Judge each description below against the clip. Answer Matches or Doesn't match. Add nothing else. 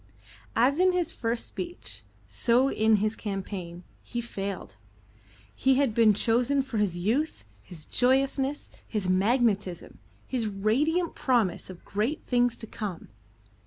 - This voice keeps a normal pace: Doesn't match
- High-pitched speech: Matches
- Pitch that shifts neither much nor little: Matches